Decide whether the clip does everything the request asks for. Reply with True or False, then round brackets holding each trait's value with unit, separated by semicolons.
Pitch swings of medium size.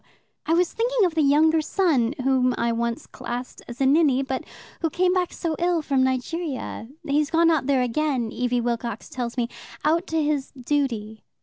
True (4.7 semitones)